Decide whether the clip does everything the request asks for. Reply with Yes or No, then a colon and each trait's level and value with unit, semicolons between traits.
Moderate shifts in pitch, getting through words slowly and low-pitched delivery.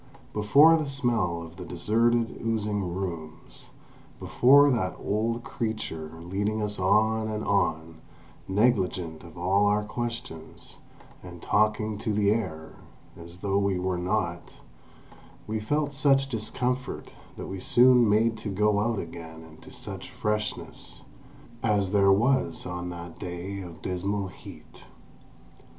Yes: average, 4.1 semitones; slow, 130 wpm; low, 105 Hz